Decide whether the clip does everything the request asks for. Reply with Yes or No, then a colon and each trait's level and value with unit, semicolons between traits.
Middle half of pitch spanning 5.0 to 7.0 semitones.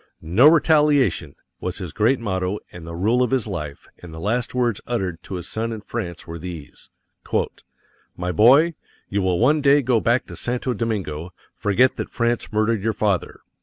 Yes: wide, 5.5 semitones